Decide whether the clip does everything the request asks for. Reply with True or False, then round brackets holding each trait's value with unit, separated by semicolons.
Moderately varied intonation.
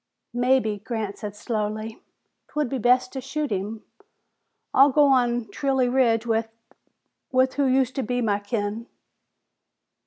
True (3.2 semitones)